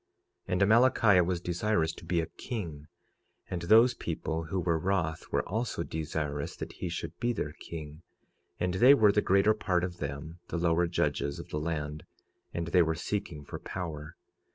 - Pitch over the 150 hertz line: No, very low, 85 Hz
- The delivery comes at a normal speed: Yes, average, 180 wpm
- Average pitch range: Yes, average, 3.6 semitones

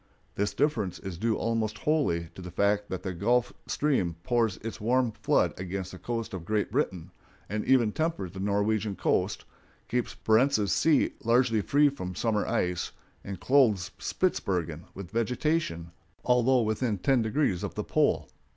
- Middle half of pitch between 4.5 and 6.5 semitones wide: Yes, average, 4.8 semitones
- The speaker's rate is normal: Yes, average, 160 wpm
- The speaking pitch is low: Yes, low, 110 Hz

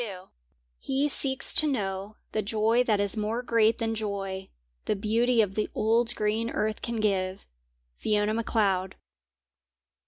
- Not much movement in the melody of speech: Yes, narrow, 2.3 semitones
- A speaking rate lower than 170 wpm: Yes, average, 145 wpm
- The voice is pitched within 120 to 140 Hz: No, high, 215 Hz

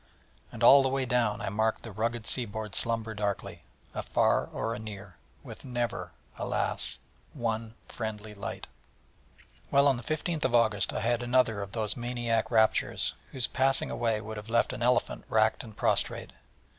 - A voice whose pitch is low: Yes, low, 115 Hz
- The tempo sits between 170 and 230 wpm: No, average, 160 wpm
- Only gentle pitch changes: Yes, narrow, 2.1 semitones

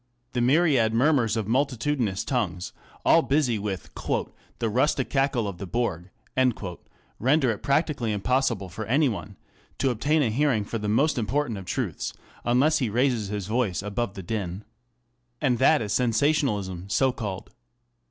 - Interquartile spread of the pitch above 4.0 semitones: Yes, average, 4.8 semitones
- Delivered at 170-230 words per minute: No, average, 155 wpm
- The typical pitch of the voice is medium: No, low, 120 Hz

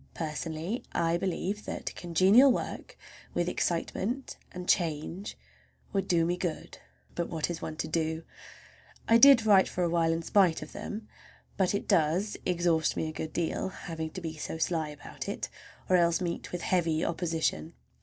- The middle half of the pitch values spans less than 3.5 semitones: Yes, average, 2.7 semitones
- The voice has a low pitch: No, medium, 170 Hz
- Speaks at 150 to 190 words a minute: Yes, average, 165 wpm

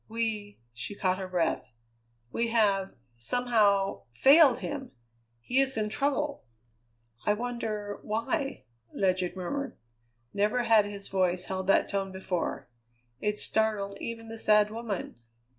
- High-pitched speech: Yes, high, 210 Hz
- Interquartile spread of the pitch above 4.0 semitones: No, average, 3.2 semitones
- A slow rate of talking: Yes, slow, 125 wpm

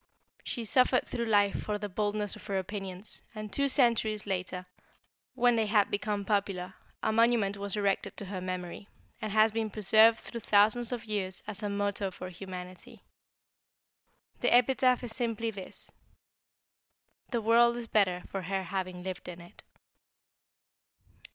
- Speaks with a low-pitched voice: No, high, 205 Hz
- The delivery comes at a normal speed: Yes, average, 150 wpm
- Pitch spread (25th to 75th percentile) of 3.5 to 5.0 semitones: No, average, 3.0 semitones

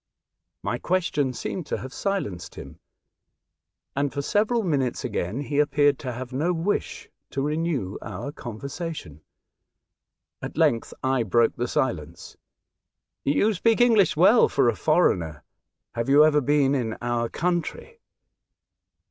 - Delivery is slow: Yes, slow, 130 wpm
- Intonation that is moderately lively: No, wide, 5.9 semitones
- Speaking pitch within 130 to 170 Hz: Yes, medium, 140 Hz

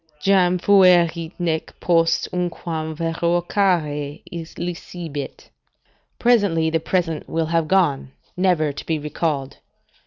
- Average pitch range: No, narrow, 2.2 semitones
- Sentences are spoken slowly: Yes, slow, 100 wpm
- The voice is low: No, medium, 165 Hz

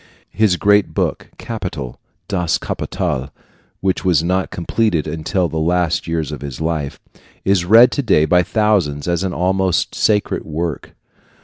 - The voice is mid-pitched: No, very low, 90 Hz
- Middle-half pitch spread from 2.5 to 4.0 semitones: Yes, average, 3.6 semitones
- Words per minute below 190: Yes, average, 145 wpm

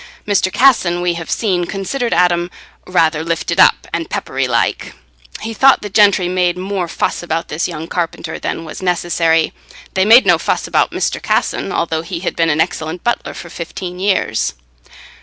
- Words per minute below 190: Yes, average, 175 wpm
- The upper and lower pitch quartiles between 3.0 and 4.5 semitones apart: No, narrow, 2.6 semitones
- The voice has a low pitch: No, medium, 175 Hz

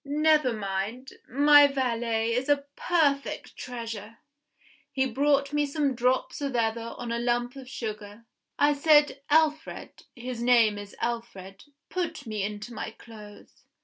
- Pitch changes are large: No, average, 4.0 semitones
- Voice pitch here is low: No, high, 245 Hz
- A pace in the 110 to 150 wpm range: Yes, average, 140 wpm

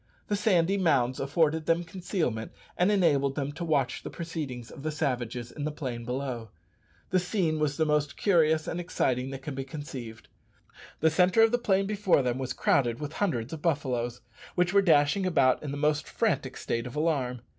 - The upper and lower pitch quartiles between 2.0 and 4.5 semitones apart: No, average, 4.9 semitones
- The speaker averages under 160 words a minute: No, average, 190 wpm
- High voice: No, medium, 150 Hz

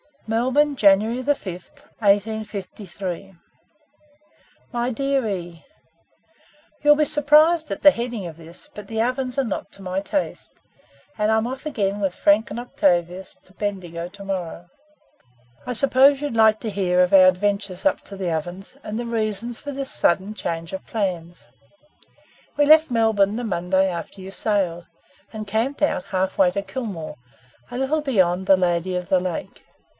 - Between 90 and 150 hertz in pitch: No, high, 205 Hz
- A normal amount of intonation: Yes, average, 4.9 semitones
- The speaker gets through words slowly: No, average, 160 wpm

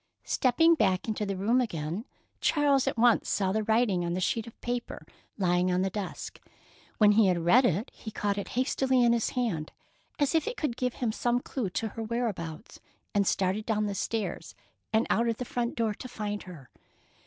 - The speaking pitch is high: Yes, high, 220 Hz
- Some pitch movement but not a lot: Yes, average, 4.1 semitones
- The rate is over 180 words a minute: Yes, average, 200 wpm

